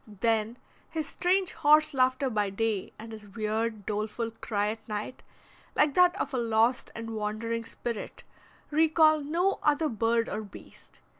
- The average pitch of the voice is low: No, high, 230 Hz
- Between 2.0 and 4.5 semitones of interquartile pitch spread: No, wide, 5.5 semitones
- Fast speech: No, average, 150 wpm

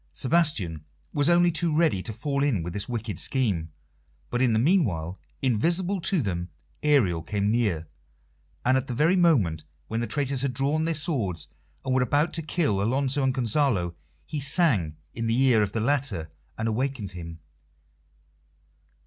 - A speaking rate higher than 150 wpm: Yes, average, 165 wpm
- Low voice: Yes, low, 125 Hz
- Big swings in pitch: Yes, wide, 6.7 semitones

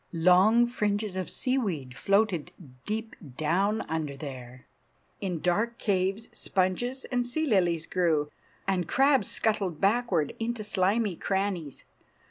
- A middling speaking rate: No, slow, 115 wpm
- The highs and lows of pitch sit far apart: No, average, 4.6 semitones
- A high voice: Yes, high, 195 Hz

